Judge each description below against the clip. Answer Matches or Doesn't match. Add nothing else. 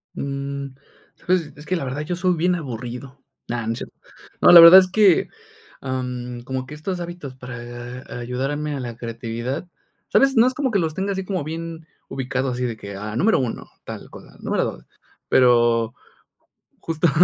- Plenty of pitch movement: Matches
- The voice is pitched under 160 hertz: Matches